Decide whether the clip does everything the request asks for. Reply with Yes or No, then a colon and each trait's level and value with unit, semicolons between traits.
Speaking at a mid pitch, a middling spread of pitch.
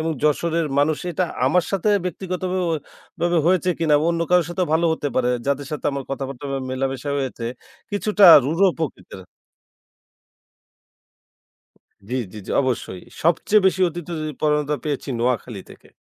Yes: medium, 155 Hz; average, 4.2 semitones